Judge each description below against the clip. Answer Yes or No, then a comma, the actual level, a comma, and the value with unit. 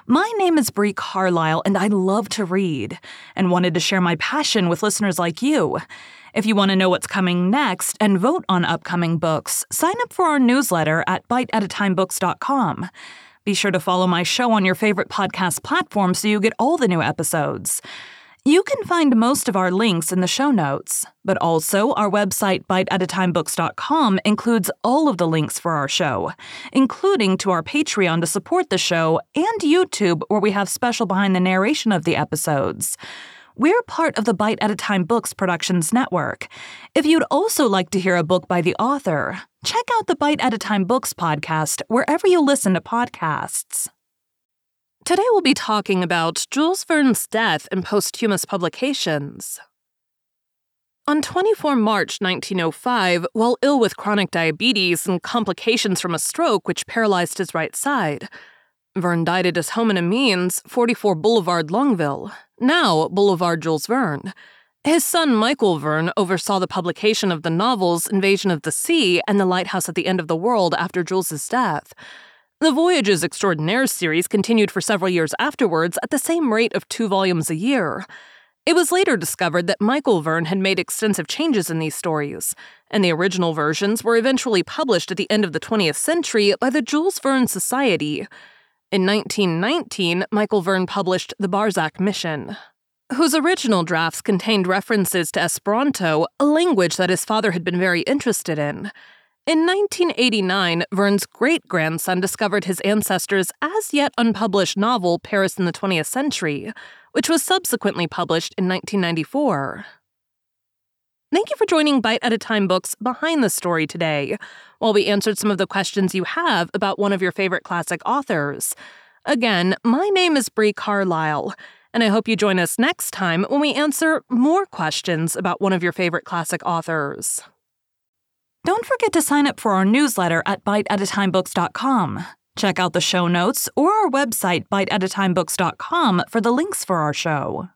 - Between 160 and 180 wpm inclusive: Yes, average, 165 wpm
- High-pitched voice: Yes, high, 200 Hz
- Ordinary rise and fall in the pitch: No, wide, 6.0 semitones